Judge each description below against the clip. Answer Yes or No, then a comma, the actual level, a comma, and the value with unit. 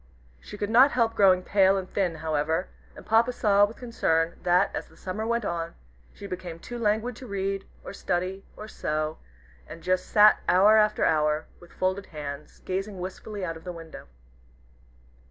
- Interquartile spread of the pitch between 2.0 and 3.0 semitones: No, average, 4.0 semitones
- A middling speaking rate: Yes, average, 175 wpm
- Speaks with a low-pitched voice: No, high, 190 Hz